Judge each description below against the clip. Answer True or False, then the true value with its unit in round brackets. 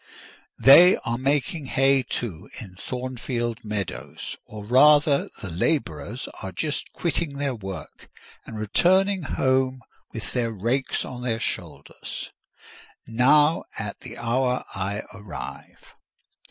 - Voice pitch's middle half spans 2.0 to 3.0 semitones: False (4.5 semitones)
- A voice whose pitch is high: False (125 Hz)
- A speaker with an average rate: False (115 wpm)